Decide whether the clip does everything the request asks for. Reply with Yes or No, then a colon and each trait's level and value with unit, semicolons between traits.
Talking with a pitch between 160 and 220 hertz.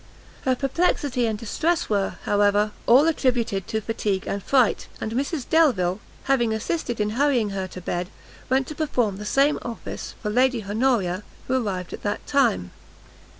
No: high, 230 Hz